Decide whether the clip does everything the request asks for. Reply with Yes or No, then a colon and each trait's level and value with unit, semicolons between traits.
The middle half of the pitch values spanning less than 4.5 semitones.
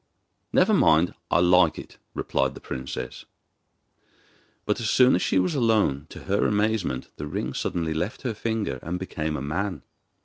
No: average, 5.2 semitones